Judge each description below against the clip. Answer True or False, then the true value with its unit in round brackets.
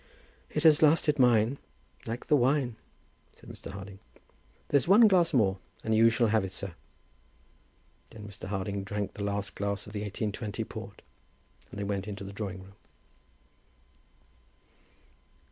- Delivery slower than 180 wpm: True (145 wpm)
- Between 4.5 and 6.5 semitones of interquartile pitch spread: False (4.1 semitones)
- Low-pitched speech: True (105 Hz)